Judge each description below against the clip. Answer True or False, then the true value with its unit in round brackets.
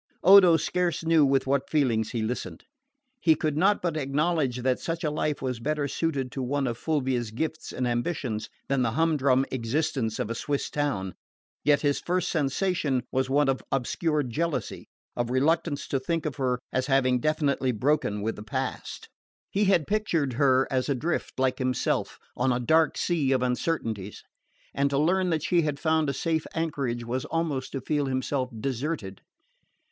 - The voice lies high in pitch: False (140 Hz)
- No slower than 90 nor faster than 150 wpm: False (175 wpm)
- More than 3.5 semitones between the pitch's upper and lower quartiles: True (3.9 semitones)